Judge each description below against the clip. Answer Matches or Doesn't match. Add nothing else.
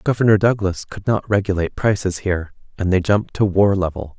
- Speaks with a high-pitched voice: Doesn't match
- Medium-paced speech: Matches